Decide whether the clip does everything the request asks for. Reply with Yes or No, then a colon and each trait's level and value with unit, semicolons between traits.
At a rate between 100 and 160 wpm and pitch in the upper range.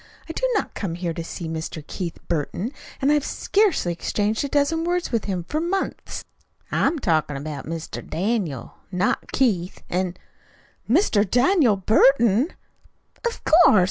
Yes: average, 150 wpm; high, 210 Hz